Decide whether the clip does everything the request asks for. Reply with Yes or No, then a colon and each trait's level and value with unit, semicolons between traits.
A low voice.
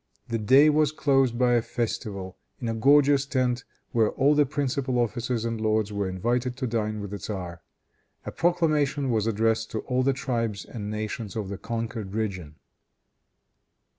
Yes: low, 115 Hz